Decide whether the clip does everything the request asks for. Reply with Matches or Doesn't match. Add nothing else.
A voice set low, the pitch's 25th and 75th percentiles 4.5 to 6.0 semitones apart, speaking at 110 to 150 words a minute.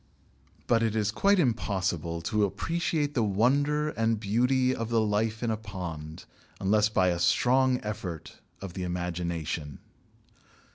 Matches